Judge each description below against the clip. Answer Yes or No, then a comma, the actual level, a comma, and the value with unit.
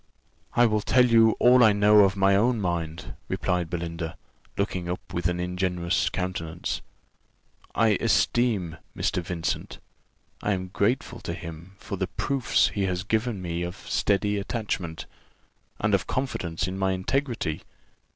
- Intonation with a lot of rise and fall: No, average, 3.7 semitones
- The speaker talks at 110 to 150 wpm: Yes, average, 145 wpm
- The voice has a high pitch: No, very low, 95 Hz